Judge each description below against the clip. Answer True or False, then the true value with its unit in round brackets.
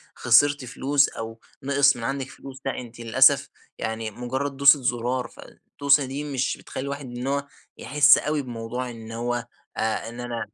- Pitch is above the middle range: False (130 Hz)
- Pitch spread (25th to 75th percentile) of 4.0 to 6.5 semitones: False (3.1 semitones)